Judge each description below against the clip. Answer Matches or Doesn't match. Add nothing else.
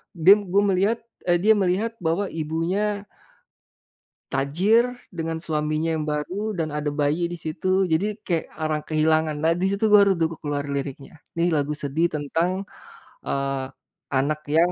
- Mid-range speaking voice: Matches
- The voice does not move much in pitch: Doesn't match